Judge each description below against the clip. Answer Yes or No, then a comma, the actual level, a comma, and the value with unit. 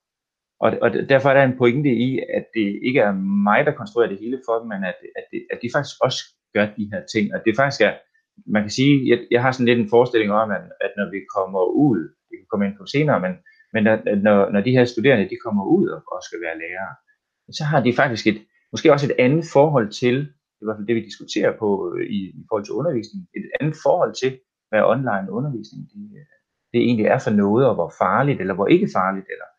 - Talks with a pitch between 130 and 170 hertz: No, low, 120 Hz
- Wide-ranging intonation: Yes, wide, 6.0 semitones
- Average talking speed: No, fast, 235 wpm